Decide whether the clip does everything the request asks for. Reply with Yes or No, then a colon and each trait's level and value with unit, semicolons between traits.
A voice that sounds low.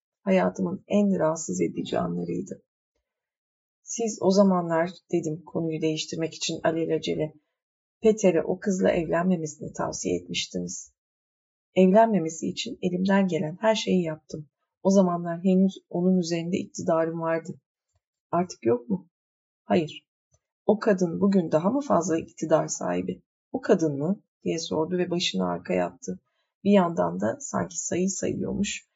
No: medium, 170 Hz